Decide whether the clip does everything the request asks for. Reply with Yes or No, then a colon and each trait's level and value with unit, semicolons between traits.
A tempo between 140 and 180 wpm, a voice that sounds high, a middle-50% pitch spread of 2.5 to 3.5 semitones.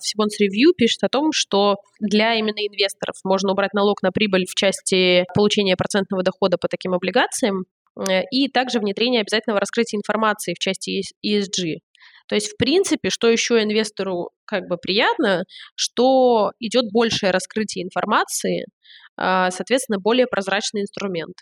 Yes: average, 145 wpm; high, 205 Hz; average, 3.1 semitones